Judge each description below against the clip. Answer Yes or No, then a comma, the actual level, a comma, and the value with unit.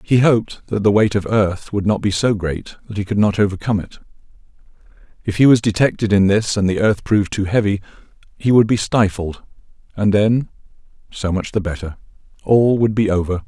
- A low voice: Yes, low, 105 Hz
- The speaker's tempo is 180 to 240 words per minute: Yes, average, 190 wpm